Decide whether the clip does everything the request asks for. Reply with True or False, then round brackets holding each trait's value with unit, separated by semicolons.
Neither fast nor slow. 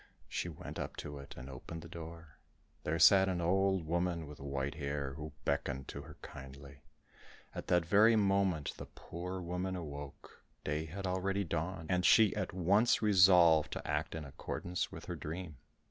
True (175 wpm)